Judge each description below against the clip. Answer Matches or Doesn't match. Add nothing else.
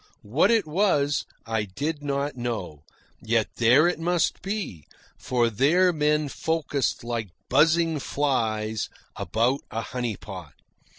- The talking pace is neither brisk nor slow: Doesn't match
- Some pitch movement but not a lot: Doesn't match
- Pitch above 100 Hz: Matches